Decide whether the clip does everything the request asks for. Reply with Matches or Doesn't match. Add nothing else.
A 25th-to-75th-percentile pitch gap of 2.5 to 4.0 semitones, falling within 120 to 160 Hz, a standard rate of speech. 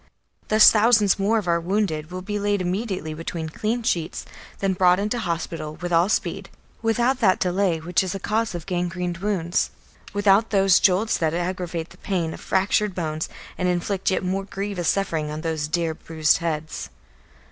Doesn't match